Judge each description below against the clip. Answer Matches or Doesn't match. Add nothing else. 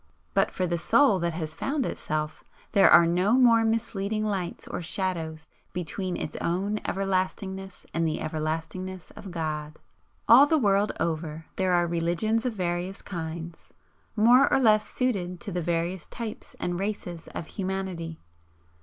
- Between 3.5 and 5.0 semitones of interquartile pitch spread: Matches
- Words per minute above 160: Doesn't match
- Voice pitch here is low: Doesn't match